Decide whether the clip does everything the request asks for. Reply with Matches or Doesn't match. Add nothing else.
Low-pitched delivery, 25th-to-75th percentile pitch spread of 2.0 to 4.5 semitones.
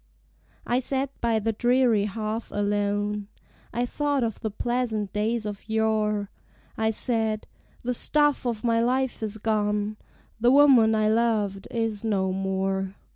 Doesn't match